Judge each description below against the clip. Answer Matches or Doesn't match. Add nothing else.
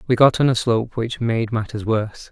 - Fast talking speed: Matches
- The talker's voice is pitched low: Matches